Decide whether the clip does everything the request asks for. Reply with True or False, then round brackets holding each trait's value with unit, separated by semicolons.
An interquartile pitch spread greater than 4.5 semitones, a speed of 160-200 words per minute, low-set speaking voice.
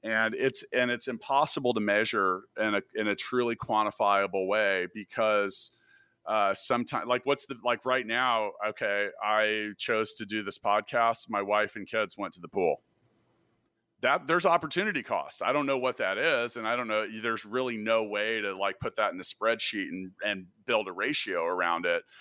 False (2.8 semitones; 190 wpm; 110 Hz)